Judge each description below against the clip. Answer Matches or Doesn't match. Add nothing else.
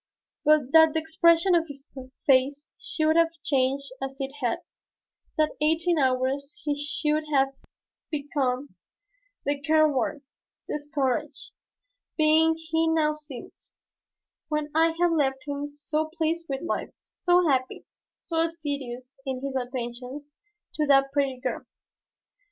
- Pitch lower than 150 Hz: Doesn't match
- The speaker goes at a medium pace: Doesn't match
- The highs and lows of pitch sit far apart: Doesn't match